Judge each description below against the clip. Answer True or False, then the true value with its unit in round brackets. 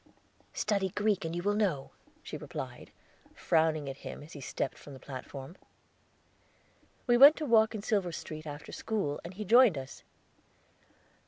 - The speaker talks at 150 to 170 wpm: True (160 wpm)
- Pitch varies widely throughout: True (6.6 semitones)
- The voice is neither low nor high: True (175 Hz)